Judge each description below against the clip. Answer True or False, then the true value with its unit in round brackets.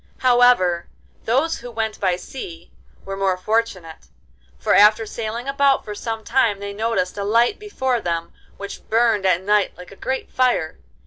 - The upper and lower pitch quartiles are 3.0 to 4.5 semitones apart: True (4.2 semitones)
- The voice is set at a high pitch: True (215 Hz)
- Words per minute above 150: True (165 wpm)